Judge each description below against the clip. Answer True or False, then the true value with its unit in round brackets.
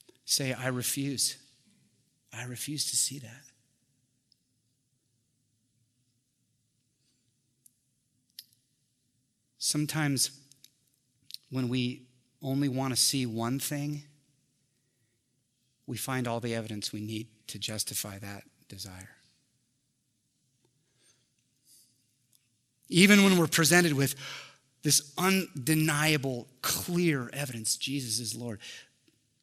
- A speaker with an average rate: False (80 wpm)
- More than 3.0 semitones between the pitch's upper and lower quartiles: False (2.4 semitones)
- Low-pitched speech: True (130 Hz)